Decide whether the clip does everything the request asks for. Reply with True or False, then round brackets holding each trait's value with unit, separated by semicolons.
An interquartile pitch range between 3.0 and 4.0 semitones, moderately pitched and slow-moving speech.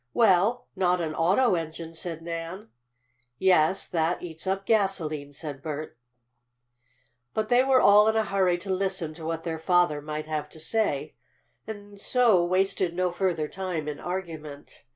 False (3.5 semitones; 175 Hz; 155 wpm)